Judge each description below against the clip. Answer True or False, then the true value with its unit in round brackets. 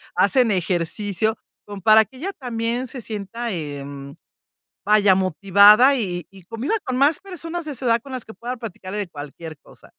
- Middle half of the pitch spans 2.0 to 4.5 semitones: False (5.2 semitones)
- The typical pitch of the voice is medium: False (215 Hz)